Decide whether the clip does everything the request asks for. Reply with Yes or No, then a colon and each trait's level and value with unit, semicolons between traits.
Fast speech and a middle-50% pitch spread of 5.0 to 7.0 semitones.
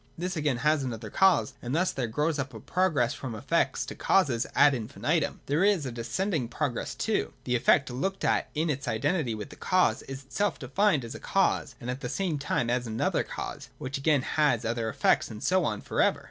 Yes: fast, 215 wpm; average, 5.3 semitones